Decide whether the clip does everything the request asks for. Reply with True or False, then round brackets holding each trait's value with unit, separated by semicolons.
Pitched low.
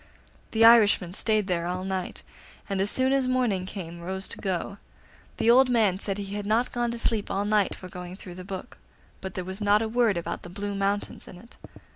False (200 Hz)